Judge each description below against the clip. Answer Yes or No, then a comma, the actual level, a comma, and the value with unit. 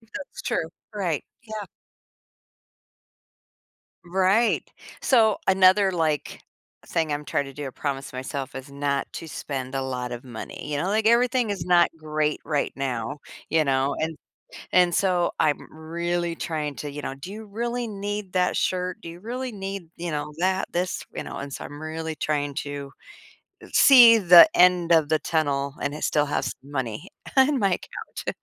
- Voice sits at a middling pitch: Yes, medium, 160 Hz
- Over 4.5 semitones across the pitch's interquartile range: Yes, average, 5.0 semitones